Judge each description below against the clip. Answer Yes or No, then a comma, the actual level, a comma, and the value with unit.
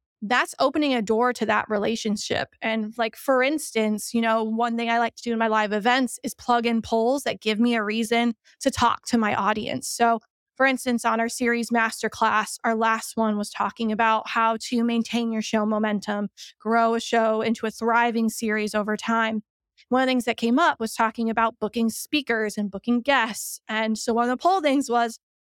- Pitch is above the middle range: Yes, high, 230 Hz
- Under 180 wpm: No, fast, 205 wpm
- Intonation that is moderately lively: No, narrow, 1.5 semitones